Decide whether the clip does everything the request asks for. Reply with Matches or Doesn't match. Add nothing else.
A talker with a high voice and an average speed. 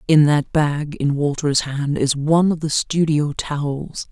Doesn't match